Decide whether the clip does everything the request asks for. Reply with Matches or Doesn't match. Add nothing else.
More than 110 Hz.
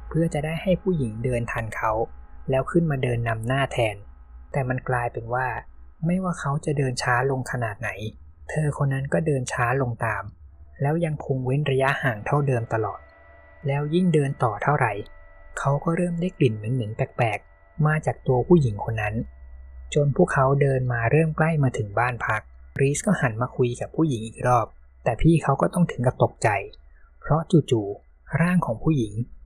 Matches